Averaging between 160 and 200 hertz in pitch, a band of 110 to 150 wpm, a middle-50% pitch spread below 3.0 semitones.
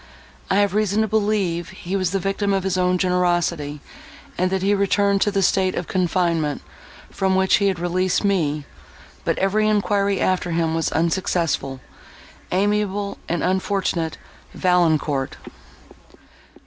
Yes: medium, 185 Hz; average, 140 wpm; narrow, 2.6 semitones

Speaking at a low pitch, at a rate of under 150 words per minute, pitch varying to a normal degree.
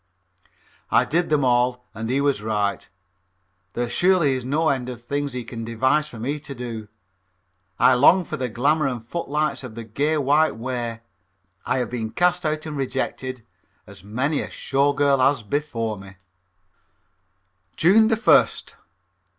No: low, 130 Hz; average, 165 wpm; average, 4.2 semitones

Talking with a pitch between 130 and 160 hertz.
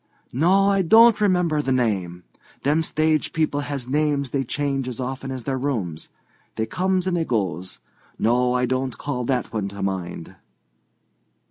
Yes: low, 135 Hz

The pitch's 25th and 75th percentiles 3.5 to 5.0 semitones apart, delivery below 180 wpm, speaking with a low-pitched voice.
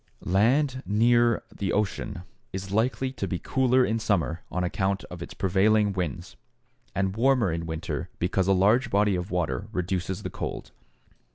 Yes: average, 4.0 semitones; average, 160 wpm; low, 100 Hz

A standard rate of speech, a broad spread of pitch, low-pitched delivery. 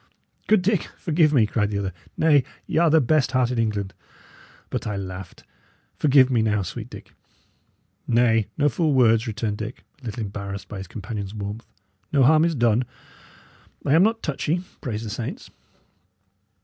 Yes: average, 170 wpm; wide, 6.0 semitones; low, 115 Hz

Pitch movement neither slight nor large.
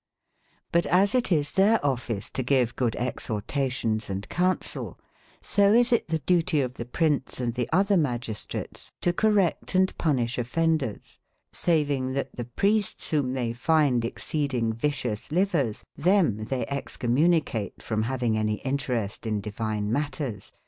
No: wide, 5.9 semitones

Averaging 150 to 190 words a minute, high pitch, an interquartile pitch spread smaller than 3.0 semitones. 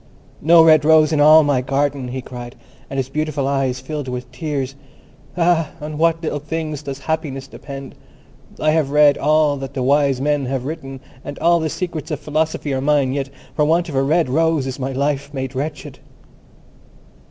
No: average, 185 wpm; medium, 145 Hz; narrow, 2.5 semitones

